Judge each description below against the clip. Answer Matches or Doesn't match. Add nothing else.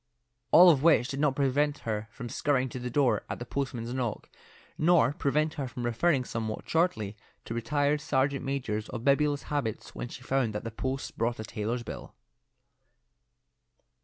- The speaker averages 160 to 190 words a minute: Matches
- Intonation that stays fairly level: Doesn't match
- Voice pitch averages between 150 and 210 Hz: Doesn't match